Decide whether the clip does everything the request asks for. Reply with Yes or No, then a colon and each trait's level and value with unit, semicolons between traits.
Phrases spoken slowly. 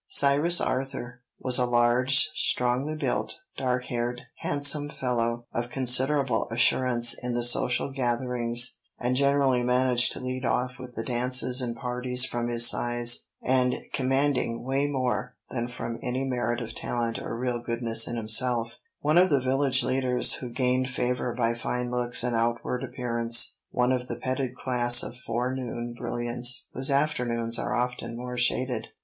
No: average, 155 wpm